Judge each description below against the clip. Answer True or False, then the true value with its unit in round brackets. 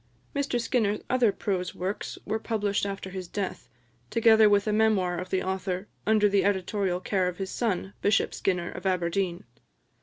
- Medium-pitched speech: False (200 Hz)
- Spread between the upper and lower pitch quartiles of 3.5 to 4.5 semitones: False (2.5 semitones)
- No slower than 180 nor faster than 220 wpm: False (170 wpm)